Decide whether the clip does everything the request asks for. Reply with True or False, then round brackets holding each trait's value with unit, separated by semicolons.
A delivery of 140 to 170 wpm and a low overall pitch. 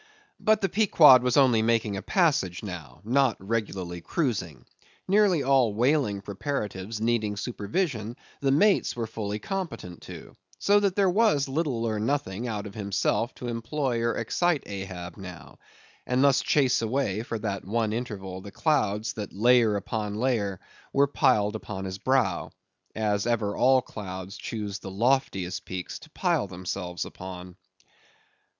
True (150 wpm; 110 Hz)